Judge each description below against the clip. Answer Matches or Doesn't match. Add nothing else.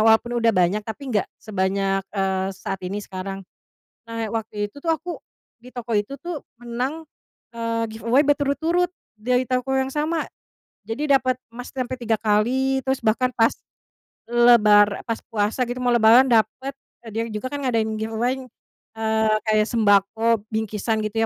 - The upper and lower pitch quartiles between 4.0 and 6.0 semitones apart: Doesn't match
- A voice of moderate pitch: Doesn't match